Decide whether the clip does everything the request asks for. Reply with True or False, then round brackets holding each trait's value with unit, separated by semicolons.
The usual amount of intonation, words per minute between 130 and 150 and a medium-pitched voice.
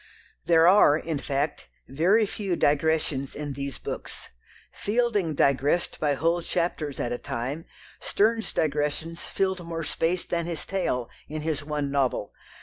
True (3.5 semitones; 145 wpm; 155 Hz)